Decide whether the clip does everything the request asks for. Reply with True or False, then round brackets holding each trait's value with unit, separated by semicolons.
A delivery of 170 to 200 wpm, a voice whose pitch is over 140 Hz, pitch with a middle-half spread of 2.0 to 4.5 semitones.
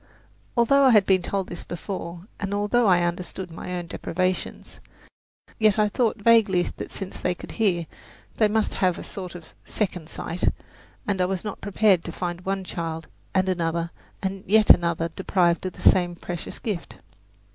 True (180 wpm; 185 Hz; 2.8 semitones)